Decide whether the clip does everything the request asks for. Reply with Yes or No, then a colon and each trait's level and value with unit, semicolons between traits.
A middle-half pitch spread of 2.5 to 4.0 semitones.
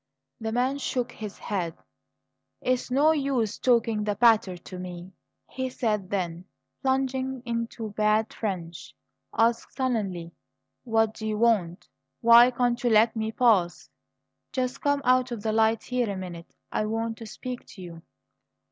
Yes: average, 3.6 semitones